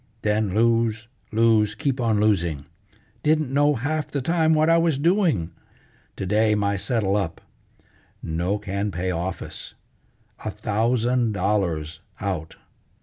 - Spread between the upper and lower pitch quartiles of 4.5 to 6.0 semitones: Yes, average, 4.9 semitones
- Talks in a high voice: No, low, 110 Hz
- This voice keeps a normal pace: No, slow, 130 wpm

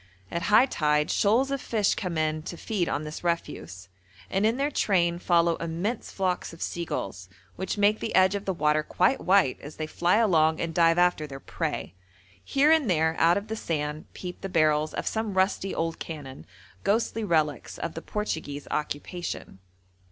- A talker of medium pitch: Yes, medium, 170 Hz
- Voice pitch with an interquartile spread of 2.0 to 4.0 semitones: No, average, 4.6 semitones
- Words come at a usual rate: Yes, average, 180 wpm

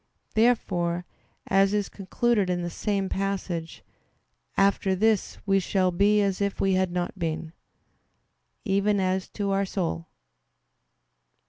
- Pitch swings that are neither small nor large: No, narrow, 1.9 semitones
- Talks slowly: Yes, slow, 125 wpm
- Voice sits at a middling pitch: No, high, 195 Hz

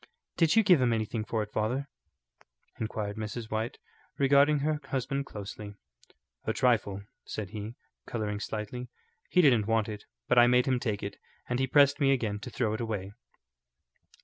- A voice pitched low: Yes, low, 115 Hz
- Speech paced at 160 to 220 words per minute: Yes, average, 170 wpm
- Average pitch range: Yes, average, 3.9 semitones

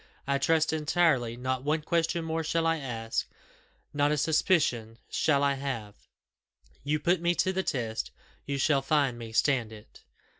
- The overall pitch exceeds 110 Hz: Yes, medium, 140 Hz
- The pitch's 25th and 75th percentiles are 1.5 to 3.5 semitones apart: No, average, 4.5 semitones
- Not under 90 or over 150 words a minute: No, average, 160 wpm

